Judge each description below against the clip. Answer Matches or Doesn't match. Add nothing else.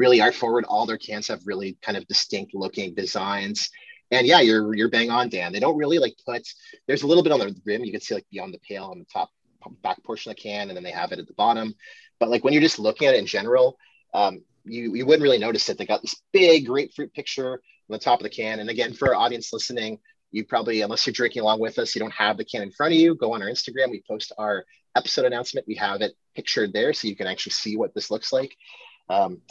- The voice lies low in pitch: Doesn't match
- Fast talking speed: Matches